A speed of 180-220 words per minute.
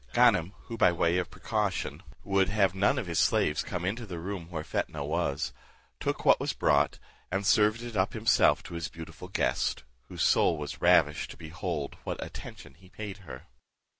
Yes: average, 185 wpm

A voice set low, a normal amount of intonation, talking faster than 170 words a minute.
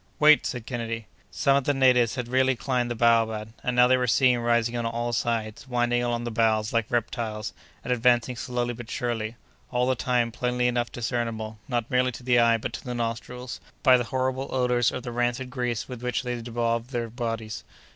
No: low, 120 Hz; narrow, 1.3 semitones; fast, 205 wpm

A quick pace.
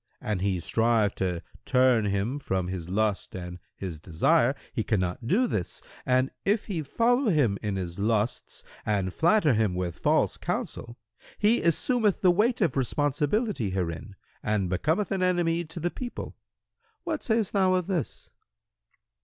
No: average, 155 wpm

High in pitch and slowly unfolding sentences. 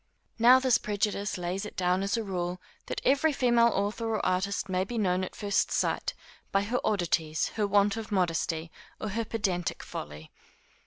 No: high, 200 Hz; average, 175 wpm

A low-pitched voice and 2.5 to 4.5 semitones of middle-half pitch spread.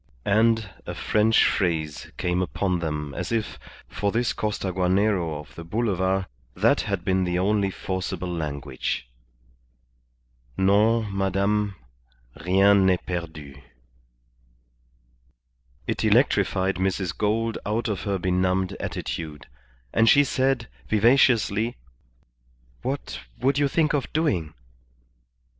Yes: very low, 95 Hz; average, 3.6 semitones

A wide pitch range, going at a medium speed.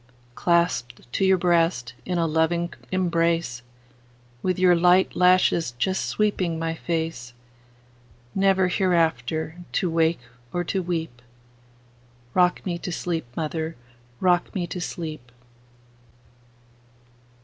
No: wide, 6.5 semitones; slow, 95 wpm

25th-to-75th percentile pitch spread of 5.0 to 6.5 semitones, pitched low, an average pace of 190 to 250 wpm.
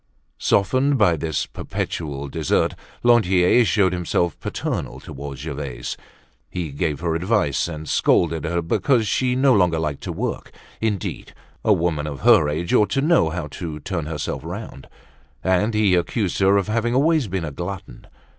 No: wide, 5.4 semitones; very low, 90 Hz; average, 160 wpm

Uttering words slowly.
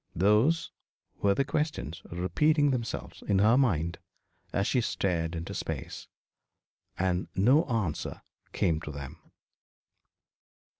Yes: slow, 110 wpm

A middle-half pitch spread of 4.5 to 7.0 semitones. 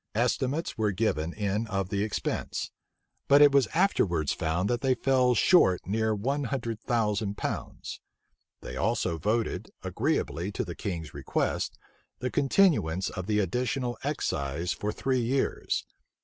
Yes: wide, 5.4 semitones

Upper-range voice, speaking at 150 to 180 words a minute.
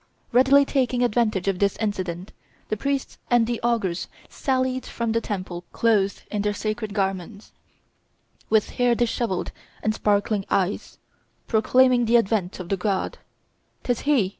No: high, 220 Hz; average, 140 wpm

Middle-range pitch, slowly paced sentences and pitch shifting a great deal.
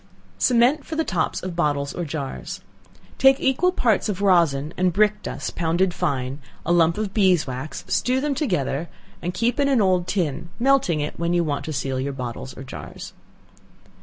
No: medium, 175 Hz; average, 180 wpm; wide, 6.7 semitones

